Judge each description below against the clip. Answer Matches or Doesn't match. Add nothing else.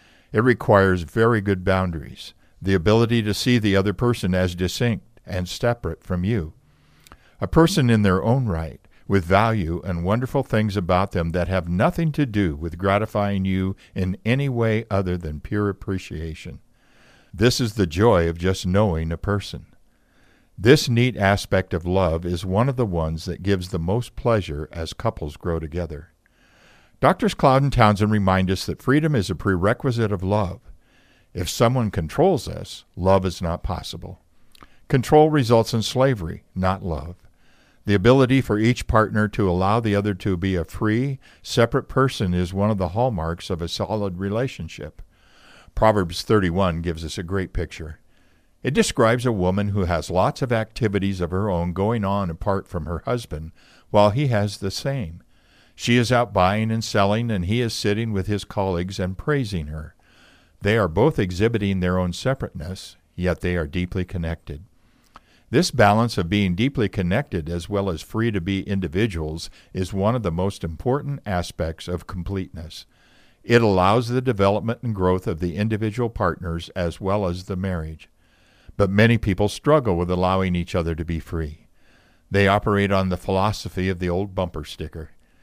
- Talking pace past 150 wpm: Matches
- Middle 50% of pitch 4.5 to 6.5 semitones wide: Doesn't match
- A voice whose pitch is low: Matches